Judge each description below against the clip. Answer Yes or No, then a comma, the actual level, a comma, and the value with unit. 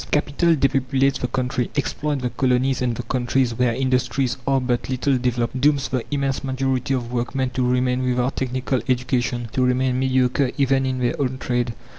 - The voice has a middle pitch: No, low, 130 Hz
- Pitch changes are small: Yes, narrow, 1.3 semitones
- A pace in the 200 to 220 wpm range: No, average, 175 wpm